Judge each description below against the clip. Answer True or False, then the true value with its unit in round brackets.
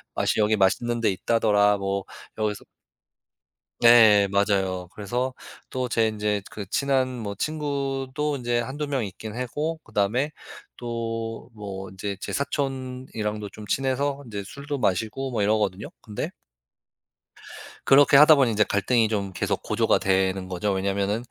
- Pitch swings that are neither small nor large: True (4.5 semitones)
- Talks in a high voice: False (110 Hz)